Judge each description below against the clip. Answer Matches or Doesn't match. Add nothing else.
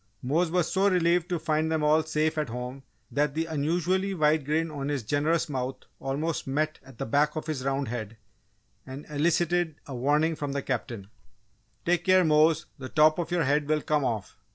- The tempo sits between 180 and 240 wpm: Matches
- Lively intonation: Doesn't match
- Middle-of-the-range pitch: Matches